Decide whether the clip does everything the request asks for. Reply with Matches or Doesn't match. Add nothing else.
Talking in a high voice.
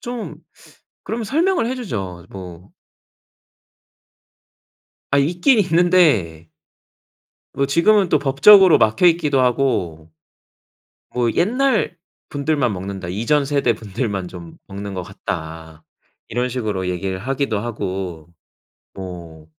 Doesn't match